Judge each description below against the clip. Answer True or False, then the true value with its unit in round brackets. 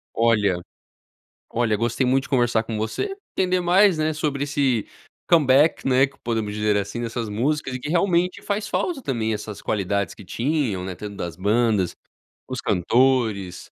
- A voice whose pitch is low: True (120 Hz)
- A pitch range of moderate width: False (5.8 semitones)